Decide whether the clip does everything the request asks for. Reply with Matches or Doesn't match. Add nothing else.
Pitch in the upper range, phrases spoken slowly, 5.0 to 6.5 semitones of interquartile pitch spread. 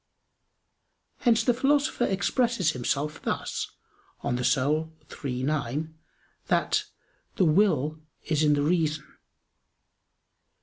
Doesn't match